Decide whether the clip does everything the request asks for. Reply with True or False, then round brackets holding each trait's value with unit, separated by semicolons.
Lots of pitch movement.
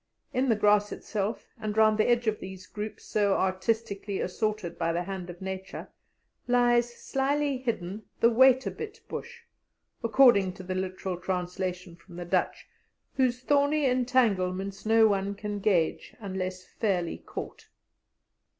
False (4.3 semitones)